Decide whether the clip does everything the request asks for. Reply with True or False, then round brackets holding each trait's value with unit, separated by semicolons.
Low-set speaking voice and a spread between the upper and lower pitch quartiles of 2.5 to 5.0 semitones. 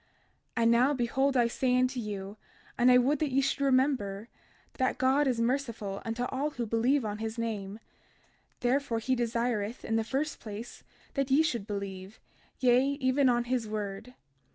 False (240 Hz; 3.2 semitones)